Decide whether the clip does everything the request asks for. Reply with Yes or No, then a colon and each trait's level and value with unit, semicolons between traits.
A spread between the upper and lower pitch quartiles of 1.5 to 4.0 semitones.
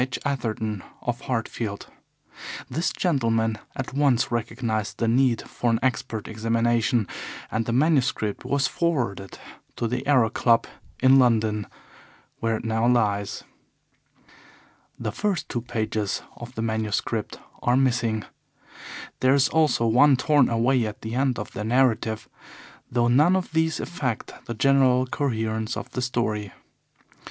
Yes: average, 3.0 semitones